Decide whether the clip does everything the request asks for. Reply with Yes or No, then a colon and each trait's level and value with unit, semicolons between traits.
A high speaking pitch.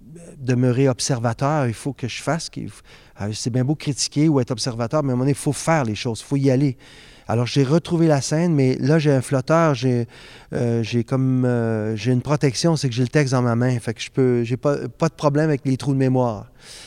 No: low, 130 Hz